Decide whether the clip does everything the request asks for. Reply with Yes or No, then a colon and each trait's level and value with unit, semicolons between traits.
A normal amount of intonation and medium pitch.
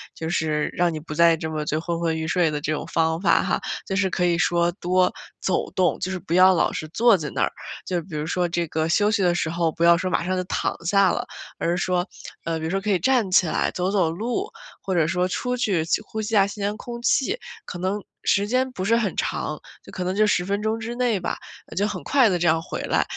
Yes: average, 3.5 semitones; medium, 180 Hz